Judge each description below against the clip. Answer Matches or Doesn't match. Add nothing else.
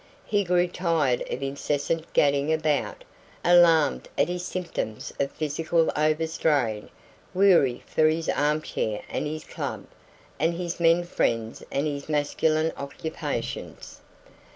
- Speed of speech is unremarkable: Doesn't match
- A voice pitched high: Doesn't match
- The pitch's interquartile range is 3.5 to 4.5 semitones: Doesn't match